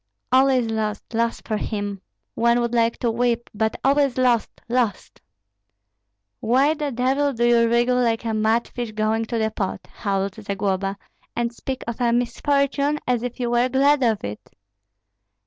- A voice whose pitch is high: Yes, high, 235 Hz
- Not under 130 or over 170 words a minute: Yes, average, 165 wpm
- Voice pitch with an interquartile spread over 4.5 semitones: No, narrow, 2.5 semitones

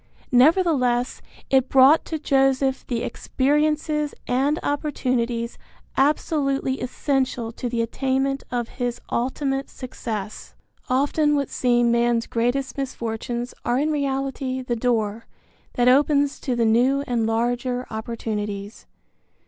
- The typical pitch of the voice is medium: No, very high, 255 Hz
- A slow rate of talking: Yes, slow, 115 wpm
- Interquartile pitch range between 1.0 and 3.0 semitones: Yes, narrow, 2.6 semitones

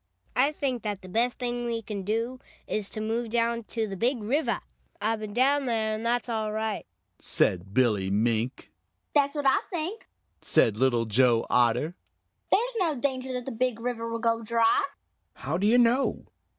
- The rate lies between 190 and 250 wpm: No, average, 180 wpm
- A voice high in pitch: Yes, high, 230 Hz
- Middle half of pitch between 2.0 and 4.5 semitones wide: Yes, average, 4.0 semitones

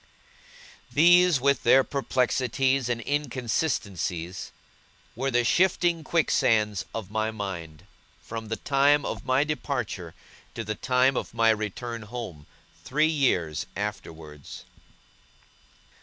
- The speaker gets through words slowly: Yes, slow, 110 wpm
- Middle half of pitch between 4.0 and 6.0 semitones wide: Yes, average, 5.0 semitones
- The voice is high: No, low, 120 Hz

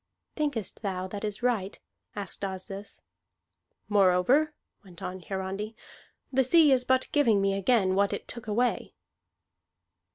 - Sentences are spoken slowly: Yes, slow, 130 wpm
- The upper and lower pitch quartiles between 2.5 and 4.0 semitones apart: No, average, 4.5 semitones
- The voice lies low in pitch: No, high, 205 Hz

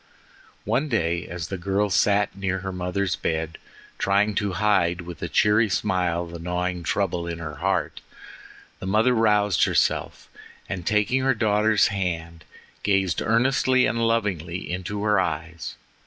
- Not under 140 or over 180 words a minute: Yes, average, 145 wpm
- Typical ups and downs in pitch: Yes, average, 3.3 semitones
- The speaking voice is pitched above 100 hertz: No, very low, 95 Hz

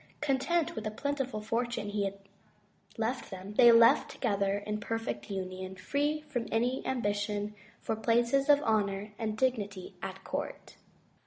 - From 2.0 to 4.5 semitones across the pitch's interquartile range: Yes, average, 3.8 semitones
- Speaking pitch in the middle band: No, high, 220 Hz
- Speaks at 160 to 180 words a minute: No, average, 150 wpm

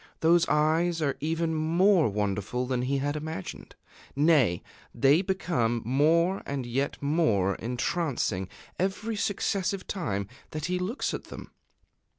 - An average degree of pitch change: No, wide, 5.8 semitones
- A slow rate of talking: Yes, slow, 130 wpm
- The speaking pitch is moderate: Yes, medium, 155 Hz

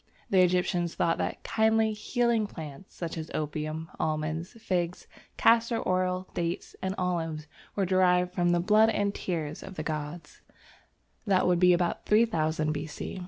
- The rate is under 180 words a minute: Yes, average, 150 wpm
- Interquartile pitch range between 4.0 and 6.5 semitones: No, average, 3.5 semitones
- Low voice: No, medium, 180 Hz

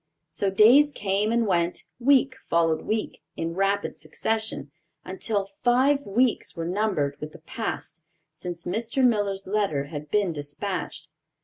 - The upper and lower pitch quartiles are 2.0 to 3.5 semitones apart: No, average, 4.9 semitones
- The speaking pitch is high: Yes, high, 200 Hz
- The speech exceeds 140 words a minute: No, slow, 135 wpm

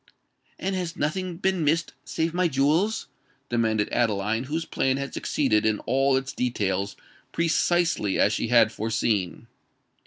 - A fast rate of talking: No, slow, 135 wpm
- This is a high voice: No, low, 135 Hz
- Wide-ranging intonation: Yes, wide, 7.1 semitones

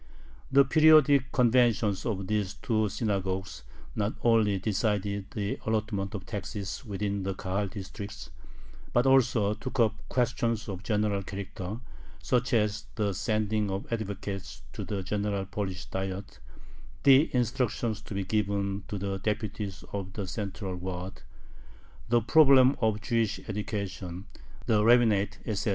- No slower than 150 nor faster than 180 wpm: No, slow, 135 wpm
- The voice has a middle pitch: No, low, 105 Hz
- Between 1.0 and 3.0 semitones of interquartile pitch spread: Yes, narrow, 2.6 semitones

